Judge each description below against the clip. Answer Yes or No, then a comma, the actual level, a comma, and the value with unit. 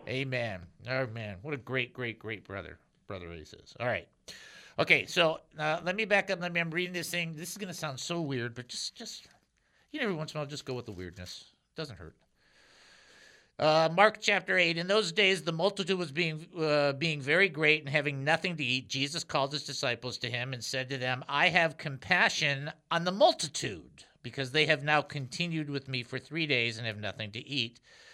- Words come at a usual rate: No, fast, 220 wpm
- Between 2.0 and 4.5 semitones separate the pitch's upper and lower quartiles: No, average, 5.1 semitones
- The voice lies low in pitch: No, medium, 150 Hz